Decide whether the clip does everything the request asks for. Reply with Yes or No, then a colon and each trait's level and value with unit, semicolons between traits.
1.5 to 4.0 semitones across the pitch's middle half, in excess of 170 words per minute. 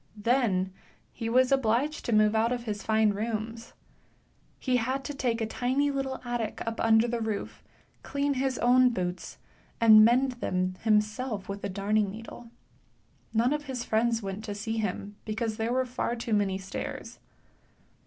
No: average, 2.8 semitones; average, 165 wpm